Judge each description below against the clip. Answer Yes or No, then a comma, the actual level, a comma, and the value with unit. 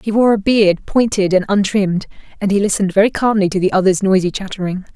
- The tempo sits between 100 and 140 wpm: No, fast, 205 wpm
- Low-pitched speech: No, high, 195 Hz